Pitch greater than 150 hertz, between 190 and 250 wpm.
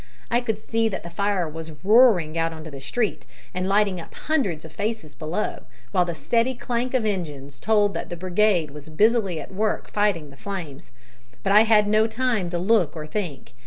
Yes: high, 190 Hz; average, 200 wpm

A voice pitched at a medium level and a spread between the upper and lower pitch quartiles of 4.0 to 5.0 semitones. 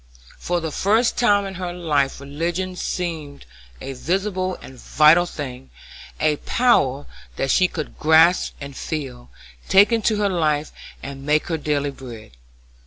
Yes: medium, 160 Hz; average, 4.7 semitones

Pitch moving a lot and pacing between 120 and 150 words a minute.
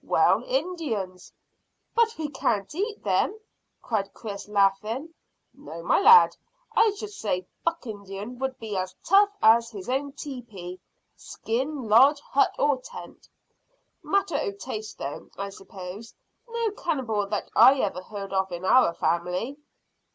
Yes: wide, 7.0 semitones; average, 140 wpm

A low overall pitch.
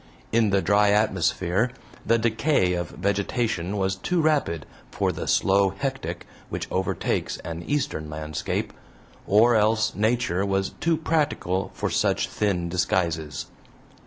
Yes: low, 100 Hz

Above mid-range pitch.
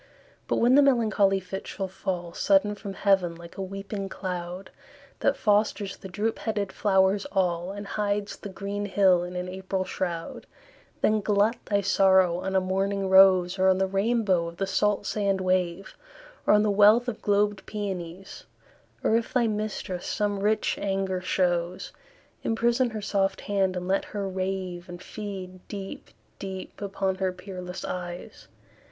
Yes: high, 195 Hz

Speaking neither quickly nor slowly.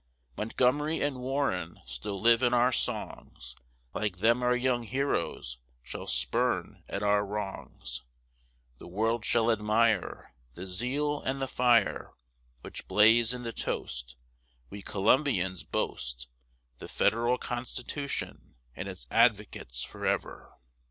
No: slow, 120 wpm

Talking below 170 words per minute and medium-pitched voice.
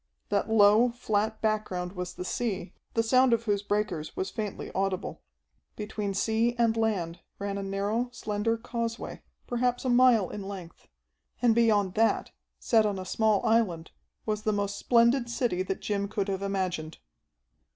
No: average, 160 wpm; high, 210 Hz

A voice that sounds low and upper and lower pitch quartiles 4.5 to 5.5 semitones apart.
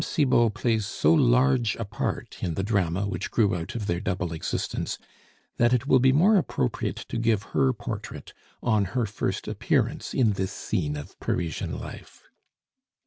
Yes: low, 110 Hz; average, 4.9 semitones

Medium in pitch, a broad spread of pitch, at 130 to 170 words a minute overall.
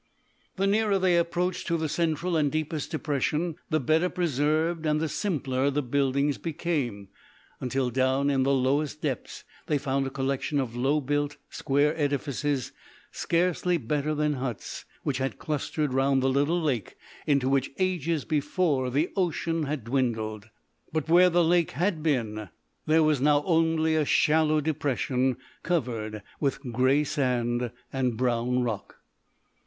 No: medium, 145 Hz; average, 3.5 semitones; average, 150 wpm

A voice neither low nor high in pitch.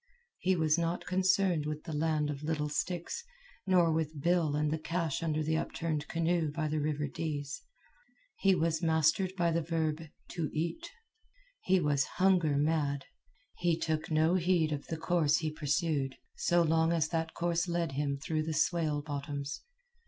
Yes: medium, 160 Hz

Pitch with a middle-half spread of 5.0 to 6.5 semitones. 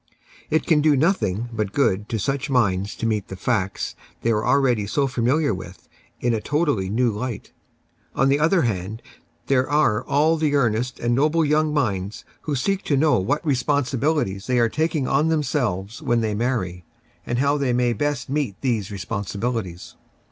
Yes: wide, 5.5 semitones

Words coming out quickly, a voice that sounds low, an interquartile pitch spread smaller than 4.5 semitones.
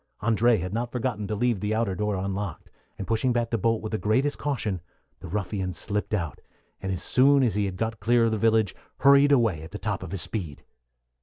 Yes: fast, 225 wpm; low, 110 Hz; average, 3.3 semitones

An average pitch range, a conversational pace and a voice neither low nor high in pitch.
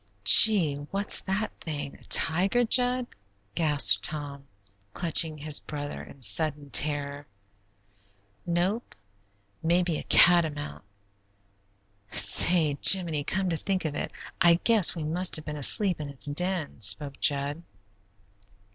No: average, 3.9 semitones; slow, 120 wpm; medium, 155 Hz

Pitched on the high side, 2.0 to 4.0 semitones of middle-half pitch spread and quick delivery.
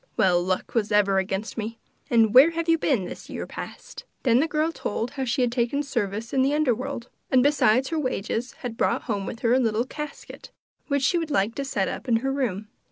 No: high, 245 Hz; average, 4.5 semitones; fast, 230 wpm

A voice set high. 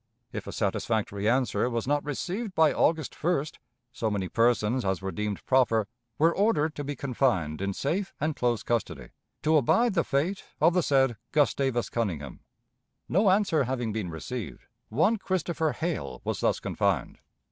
No: low, 135 Hz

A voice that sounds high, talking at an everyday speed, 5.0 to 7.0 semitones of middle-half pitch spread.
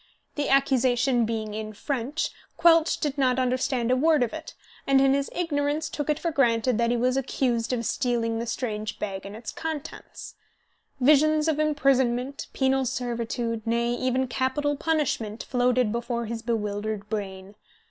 No: very high, 250 Hz; average, 160 wpm; average, 3.5 semitones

